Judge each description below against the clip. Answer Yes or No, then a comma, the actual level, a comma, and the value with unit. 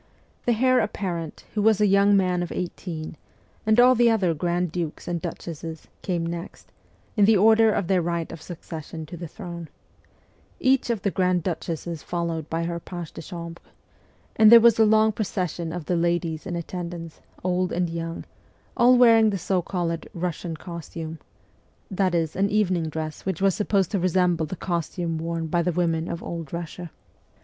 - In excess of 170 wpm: Yes, average, 180 wpm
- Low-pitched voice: No, medium, 175 Hz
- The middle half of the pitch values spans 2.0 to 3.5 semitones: Yes, average, 3.0 semitones